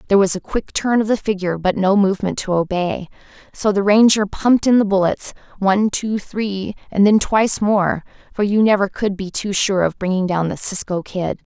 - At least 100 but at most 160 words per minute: No, average, 190 wpm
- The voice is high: Yes, high, 200 Hz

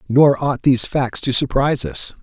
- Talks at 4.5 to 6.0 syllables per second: Yes, 5.0 syllables/s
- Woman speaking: No, male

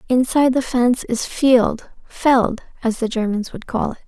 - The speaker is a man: No, female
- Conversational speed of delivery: Yes, average, 160 wpm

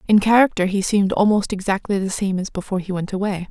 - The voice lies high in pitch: Yes, high, 195 Hz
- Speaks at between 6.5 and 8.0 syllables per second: Yes, 6.6 syllables/s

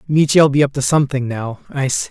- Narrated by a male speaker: Yes, male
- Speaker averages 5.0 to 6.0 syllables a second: Yes, 5.9 syllables/s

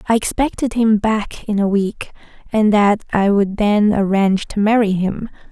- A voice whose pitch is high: Yes, high, 210 Hz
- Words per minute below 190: Yes, average, 175 wpm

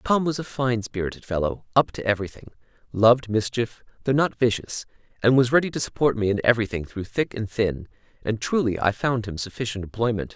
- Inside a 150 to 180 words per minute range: No, average, 190 wpm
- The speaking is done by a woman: No, male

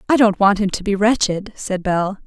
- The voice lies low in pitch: No, high, 200 Hz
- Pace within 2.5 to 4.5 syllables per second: No, 5.0 syllables/s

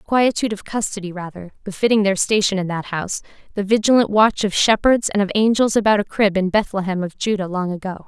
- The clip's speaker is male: No, female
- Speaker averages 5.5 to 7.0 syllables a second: Yes, 6.0 syllables/s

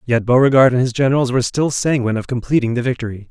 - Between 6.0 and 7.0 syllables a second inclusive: No, 7.2 syllables/s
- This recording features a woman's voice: No, male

